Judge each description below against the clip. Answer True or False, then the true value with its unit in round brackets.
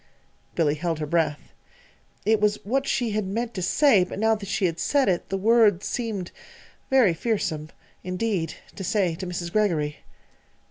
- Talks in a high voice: True (195 Hz)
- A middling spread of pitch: True (4.4 semitones)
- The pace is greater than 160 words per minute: True (170 wpm)